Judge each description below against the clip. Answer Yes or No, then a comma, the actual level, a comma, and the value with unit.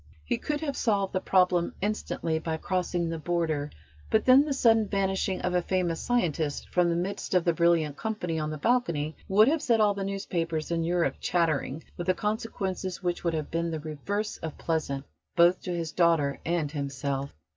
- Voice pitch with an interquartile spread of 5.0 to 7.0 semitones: No, average, 3.7 semitones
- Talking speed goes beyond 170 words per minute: Yes, average, 190 wpm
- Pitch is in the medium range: Yes, medium, 175 Hz